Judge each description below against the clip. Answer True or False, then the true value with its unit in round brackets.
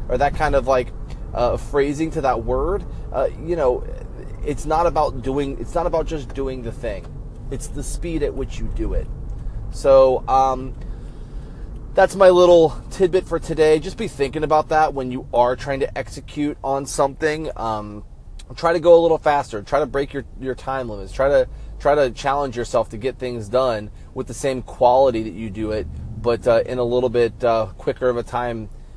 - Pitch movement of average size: True (4.4 semitones)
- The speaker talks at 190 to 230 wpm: True (200 wpm)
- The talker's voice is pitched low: True (130 Hz)